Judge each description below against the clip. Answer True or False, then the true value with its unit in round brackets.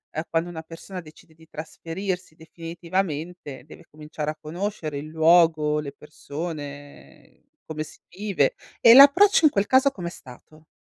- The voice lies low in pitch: False (165 Hz)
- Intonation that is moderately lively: True (3.2 semitones)